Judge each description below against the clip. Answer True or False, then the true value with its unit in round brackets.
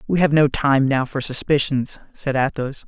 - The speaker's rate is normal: True (190 wpm)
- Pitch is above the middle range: False (140 Hz)